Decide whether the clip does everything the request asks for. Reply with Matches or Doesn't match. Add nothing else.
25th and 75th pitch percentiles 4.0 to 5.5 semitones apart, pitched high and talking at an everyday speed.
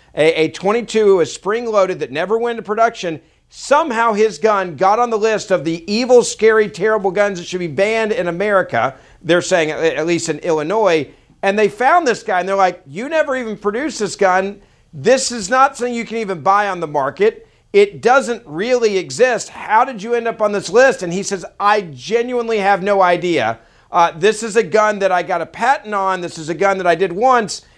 Doesn't match